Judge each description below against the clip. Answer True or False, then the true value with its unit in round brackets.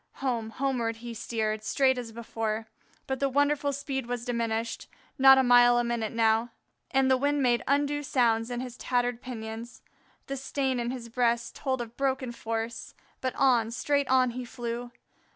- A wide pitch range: False (2.4 semitones)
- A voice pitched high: True (245 Hz)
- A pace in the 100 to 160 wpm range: False (170 wpm)